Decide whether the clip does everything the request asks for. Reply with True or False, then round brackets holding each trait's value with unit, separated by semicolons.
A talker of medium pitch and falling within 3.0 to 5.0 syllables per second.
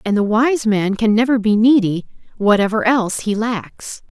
False (220 Hz; 4.7 syllables/s)